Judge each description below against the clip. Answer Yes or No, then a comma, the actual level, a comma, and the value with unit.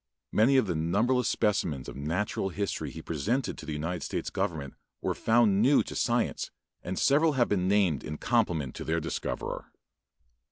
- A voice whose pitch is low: Yes, very low, 95 Hz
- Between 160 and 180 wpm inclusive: Yes, average, 170 wpm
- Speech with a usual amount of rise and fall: No, wide, 6.7 semitones